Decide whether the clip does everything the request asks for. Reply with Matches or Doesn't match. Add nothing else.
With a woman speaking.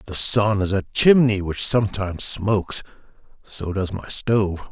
Doesn't match